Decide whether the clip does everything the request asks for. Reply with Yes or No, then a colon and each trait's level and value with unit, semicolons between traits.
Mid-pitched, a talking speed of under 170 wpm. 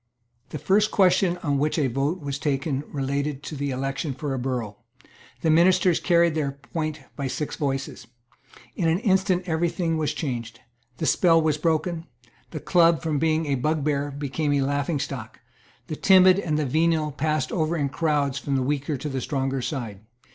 No: medium, 150 Hz; average, 175 wpm